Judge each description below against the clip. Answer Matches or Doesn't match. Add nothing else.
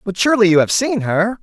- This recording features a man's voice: Matches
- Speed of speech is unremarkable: Doesn't match